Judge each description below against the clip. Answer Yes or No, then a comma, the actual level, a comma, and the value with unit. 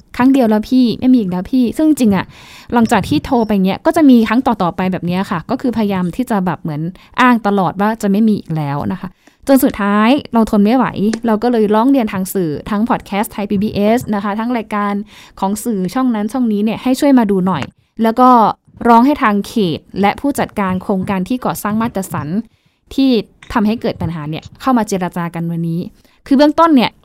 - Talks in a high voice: Yes, high, 215 Hz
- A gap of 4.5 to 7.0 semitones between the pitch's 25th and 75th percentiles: No, average, 3.9 semitones